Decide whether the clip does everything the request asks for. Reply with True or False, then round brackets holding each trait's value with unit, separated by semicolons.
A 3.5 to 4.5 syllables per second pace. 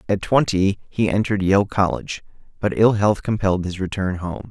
False (5.4 syllables/s)